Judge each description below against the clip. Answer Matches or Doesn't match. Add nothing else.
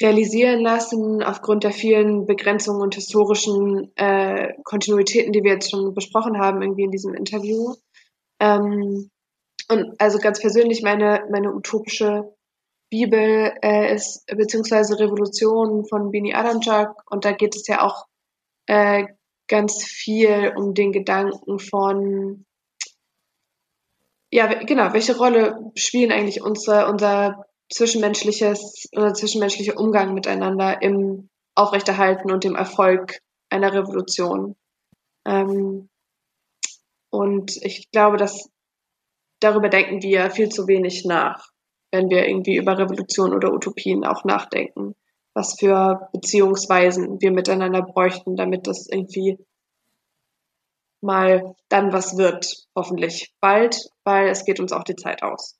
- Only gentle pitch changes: Matches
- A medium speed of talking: Doesn't match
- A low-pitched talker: Doesn't match